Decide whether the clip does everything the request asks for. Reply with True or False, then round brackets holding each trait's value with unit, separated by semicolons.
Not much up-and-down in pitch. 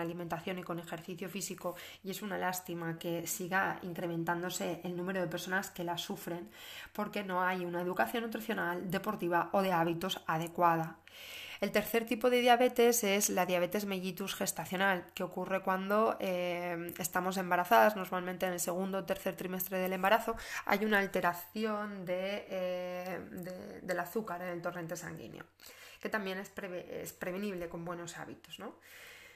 True (2.0 semitones)